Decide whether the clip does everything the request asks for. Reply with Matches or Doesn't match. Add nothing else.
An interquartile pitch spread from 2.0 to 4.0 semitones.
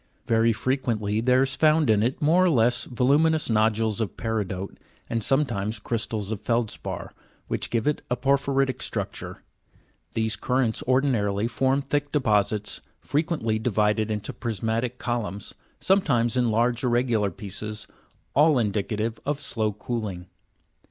Matches